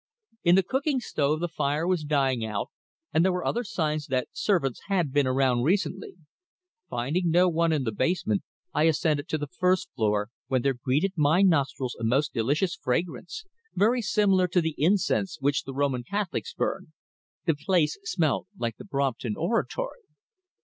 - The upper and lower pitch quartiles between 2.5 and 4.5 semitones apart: No, average, 5.3 semitones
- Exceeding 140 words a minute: Yes, average, 170 wpm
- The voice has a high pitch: No, medium, 155 Hz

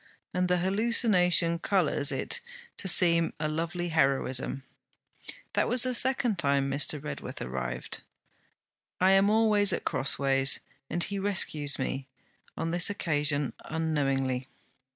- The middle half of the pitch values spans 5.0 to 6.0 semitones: Yes, wide, 5.6 semitones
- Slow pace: Yes, slow, 125 wpm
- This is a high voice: No, medium, 165 Hz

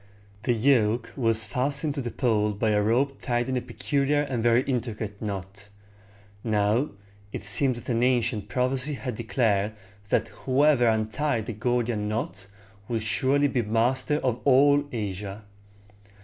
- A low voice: Yes, low, 120 Hz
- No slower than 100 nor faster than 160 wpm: Yes, average, 150 wpm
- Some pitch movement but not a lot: Yes, average, 3.5 semitones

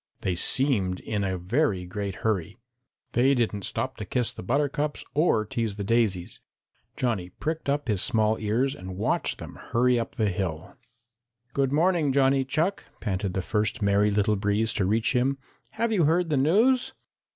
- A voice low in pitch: Yes, low, 115 Hz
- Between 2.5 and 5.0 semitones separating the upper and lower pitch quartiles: No, wide, 5.6 semitones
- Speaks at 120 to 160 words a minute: No, average, 170 wpm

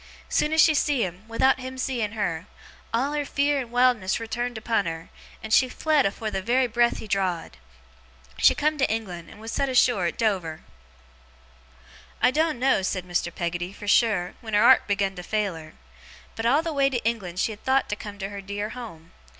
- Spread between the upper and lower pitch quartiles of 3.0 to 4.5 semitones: No, average, 5.1 semitones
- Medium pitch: No, high, 220 Hz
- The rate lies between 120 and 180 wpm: No, fast, 205 wpm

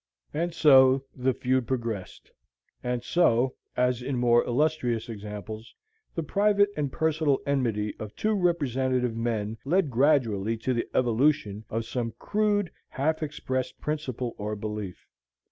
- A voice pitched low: Yes, low, 130 Hz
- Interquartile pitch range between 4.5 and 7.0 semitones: Yes, average, 4.8 semitones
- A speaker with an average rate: No, slow, 130 wpm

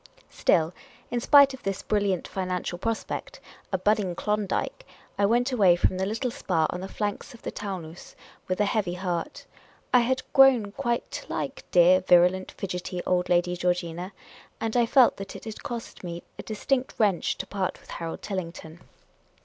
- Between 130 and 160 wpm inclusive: No, average, 175 wpm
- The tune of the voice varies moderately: Yes, average, 4.3 semitones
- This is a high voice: Yes, high, 195 Hz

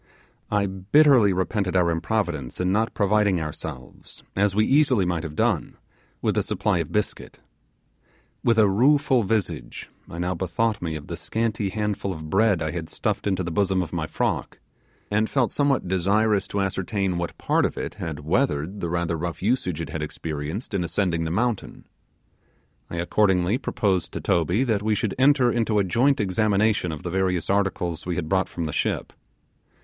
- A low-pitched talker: Yes, very low, 95 Hz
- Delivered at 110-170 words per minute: No, average, 180 wpm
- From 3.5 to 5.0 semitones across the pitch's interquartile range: Yes, average, 4.0 semitones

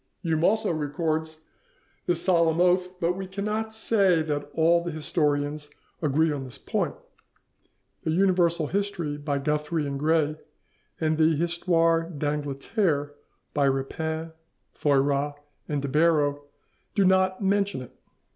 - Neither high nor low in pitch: Yes, medium, 160 Hz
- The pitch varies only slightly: No, average, 3.4 semitones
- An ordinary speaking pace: No, slow, 125 wpm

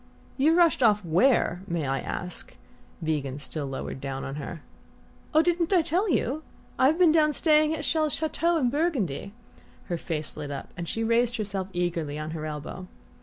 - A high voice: Yes, high, 205 Hz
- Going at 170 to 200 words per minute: Yes, average, 180 wpm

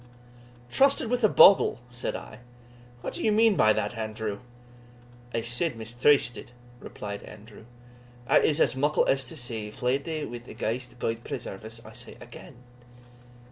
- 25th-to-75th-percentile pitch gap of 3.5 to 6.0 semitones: Yes, average, 4.9 semitones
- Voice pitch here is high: No, low, 120 Hz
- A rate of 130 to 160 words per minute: Yes, average, 155 wpm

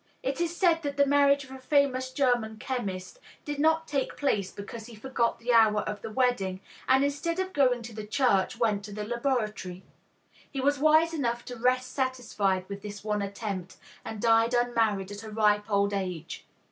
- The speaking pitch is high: Yes, high, 240 Hz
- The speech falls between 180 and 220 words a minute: Yes, average, 190 wpm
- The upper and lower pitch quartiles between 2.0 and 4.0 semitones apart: No, average, 4.8 semitones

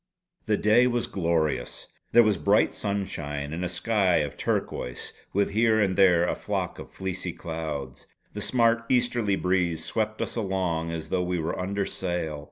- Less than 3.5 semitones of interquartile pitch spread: No, average, 4.3 semitones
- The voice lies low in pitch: Yes, very low, 95 Hz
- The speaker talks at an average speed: Yes, average, 170 wpm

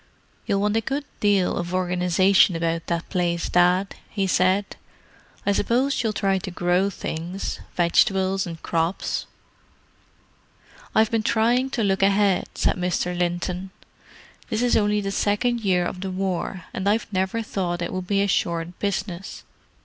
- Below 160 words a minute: Yes, average, 150 wpm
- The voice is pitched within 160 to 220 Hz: Yes, high, 190 Hz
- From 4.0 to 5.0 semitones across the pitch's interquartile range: No, narrow, 2.5 semitones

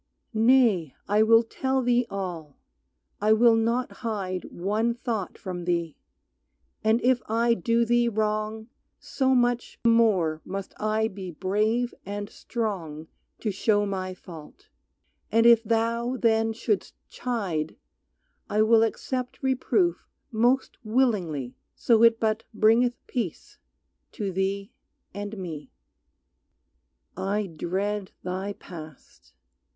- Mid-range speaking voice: No, high, 215 Hz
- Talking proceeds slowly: Yes, slow, 120 wpm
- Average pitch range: Yes, average, 3.7 semitones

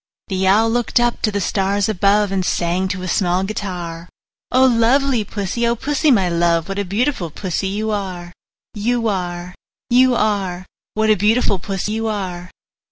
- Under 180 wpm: Yes, average, 170 wpm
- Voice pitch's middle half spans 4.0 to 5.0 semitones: No, average, 3.6 semitones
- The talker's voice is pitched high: Yes, high, 200 Hz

